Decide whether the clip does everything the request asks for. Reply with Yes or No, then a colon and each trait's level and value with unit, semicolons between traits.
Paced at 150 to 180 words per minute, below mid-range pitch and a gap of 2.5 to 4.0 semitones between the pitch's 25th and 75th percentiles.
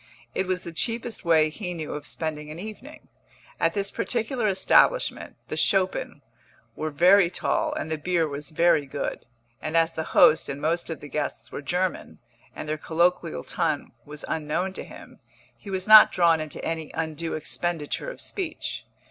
No: average, 175 wpm; medium, 165 Hz; average, 3.5 semitones